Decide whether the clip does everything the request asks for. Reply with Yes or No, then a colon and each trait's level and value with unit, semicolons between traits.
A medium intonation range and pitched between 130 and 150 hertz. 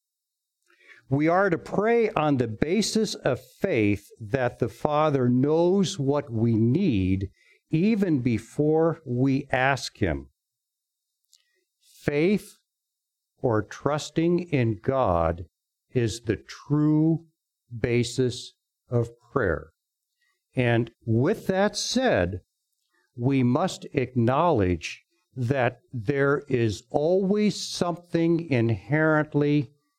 No: wide, 6.3 semitones; medium, 140 Hz